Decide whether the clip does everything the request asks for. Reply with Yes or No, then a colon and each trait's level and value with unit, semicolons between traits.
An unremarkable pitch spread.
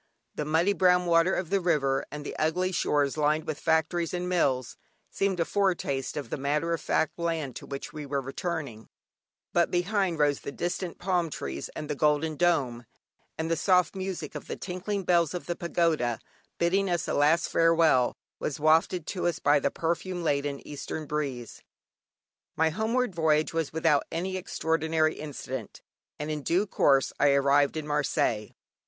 Yes: average, 3.3 semitones